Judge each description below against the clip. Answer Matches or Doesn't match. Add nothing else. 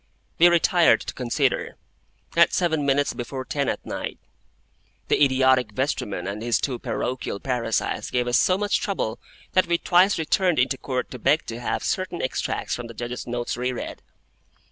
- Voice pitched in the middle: Doesn't match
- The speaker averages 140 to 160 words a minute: Doesn't match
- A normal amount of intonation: Doesn't match